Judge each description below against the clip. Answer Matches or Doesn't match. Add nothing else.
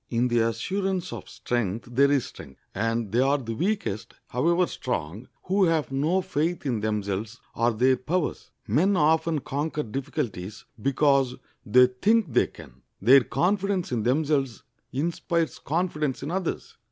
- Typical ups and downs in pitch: Doesn't match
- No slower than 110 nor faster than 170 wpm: Matches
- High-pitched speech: Doesn't match